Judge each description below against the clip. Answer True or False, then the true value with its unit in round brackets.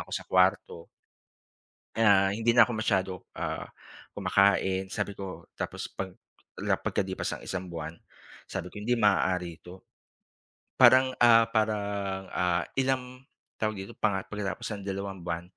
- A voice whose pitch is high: False (100 Hz)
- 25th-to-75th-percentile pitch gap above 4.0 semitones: False (2.7 semitones)